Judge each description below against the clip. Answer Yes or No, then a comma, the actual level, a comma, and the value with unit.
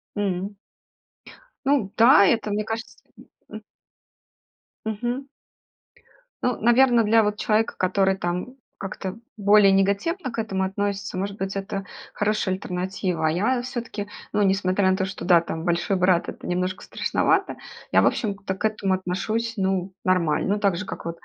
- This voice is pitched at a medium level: No, high, 195 Hz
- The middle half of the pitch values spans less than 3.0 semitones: Yes, narrow, 2.5 semitones